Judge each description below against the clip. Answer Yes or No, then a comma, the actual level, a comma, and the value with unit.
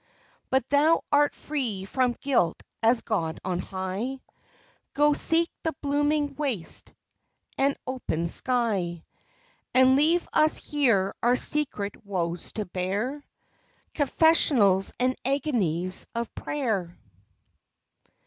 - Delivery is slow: Yes, slow, 105 wpm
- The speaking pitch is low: No, very high, 250 Hz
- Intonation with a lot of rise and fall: Yes, wide, 7.1 semitones